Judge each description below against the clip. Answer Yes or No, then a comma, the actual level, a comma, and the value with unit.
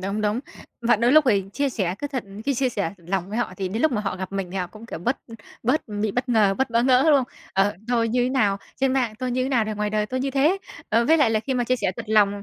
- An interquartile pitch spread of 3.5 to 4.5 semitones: Yes, average, 4.1 semitones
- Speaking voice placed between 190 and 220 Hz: No, high, 230 Hz